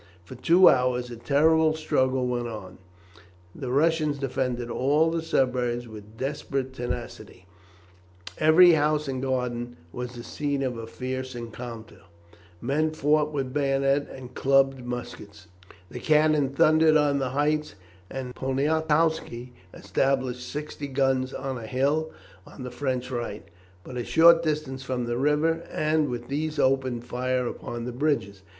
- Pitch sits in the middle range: No, low, 130 Hz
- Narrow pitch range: No, average, 3.3 semitones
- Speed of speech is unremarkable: Yes, average, 145 wpm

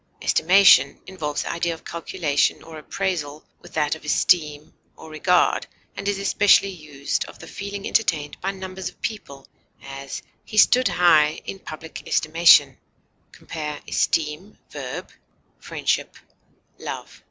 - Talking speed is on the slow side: Yes, slow, 130 wpm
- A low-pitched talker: No, medium, 165 Hz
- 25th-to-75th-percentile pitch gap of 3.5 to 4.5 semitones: Yes, average, 4.1 semitones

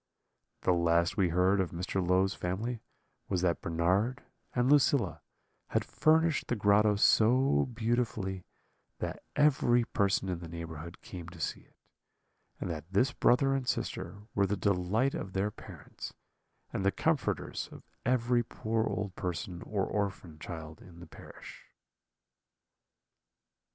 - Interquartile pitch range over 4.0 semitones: Yes, average, 5.2 semitones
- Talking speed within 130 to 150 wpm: Yes, average, 140 wpm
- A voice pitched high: No, low, 100 Hz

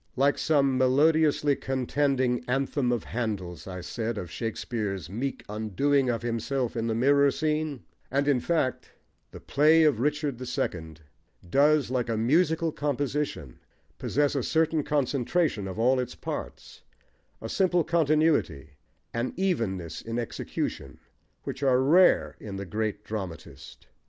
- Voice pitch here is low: Yes, low, 130 Hz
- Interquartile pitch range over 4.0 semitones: Yes, average, 4.9 semitones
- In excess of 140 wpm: No, slow, 135 wpm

